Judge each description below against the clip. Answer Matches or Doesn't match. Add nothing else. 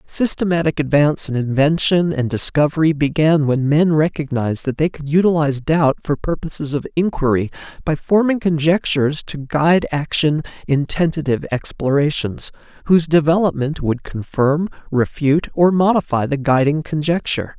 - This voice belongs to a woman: Doesn't match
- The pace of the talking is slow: Matches